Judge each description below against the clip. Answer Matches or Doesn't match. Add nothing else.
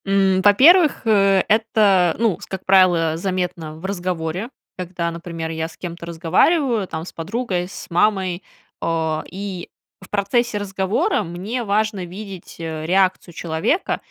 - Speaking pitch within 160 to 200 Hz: Matches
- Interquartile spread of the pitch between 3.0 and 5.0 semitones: Matches